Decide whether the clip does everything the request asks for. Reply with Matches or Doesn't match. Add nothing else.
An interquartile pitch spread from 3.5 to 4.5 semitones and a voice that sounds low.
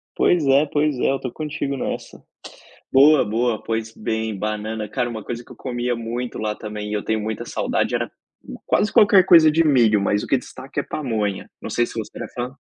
Matches